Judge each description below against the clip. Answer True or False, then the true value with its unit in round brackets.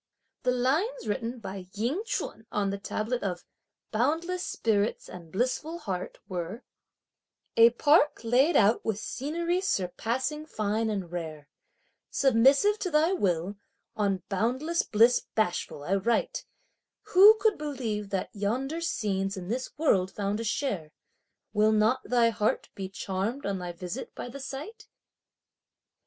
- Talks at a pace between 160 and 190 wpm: False (140 wpm)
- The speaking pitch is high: True (225 Hz)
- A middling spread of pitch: False (6.0 semitones)